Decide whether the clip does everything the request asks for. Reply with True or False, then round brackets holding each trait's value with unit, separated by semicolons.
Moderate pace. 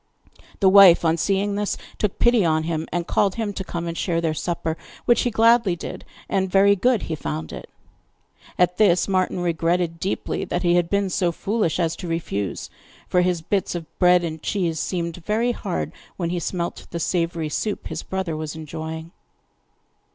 True (185 wpm)